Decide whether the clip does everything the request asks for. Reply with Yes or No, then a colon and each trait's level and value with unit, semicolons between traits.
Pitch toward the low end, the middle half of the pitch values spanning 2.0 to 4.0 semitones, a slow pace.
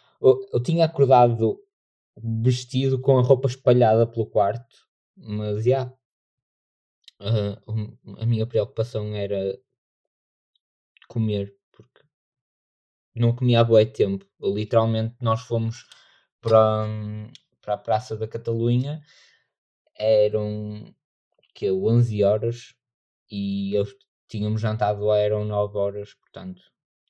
Yes: low, 110 Hz; average, 3.1 semitones; slow, 110 wpm